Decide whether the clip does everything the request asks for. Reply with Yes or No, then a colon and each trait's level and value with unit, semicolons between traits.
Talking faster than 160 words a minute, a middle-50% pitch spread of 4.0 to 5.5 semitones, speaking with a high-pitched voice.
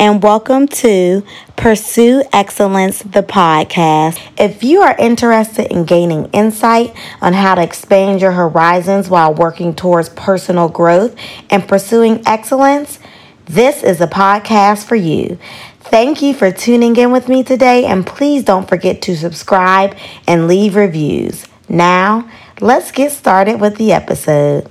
No: average, 140 wpm; average, 4.4 semitones; high, 200 Hz